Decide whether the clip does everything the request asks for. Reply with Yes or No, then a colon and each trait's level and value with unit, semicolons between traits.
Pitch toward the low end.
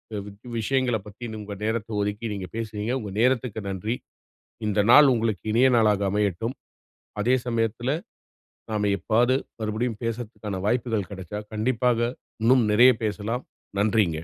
Yes: low, 110 Hz